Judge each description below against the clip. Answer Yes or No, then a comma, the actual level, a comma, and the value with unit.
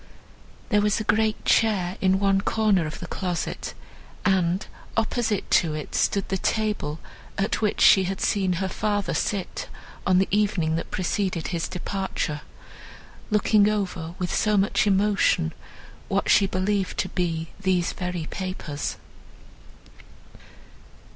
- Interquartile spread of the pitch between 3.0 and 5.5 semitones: No, narrow, 2.6 semitones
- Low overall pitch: No, high, 190 Hz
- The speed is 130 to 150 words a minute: Yes, slow, 135 wpm